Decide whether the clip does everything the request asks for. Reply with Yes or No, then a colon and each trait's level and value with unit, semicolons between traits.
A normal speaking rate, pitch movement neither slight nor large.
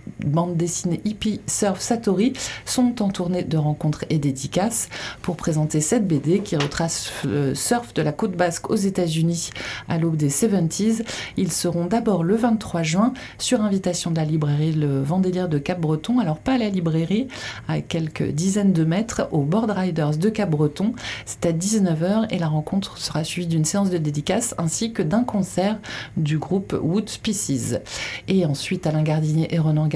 Yes: average, 175 wpm; average, 4.6 semitones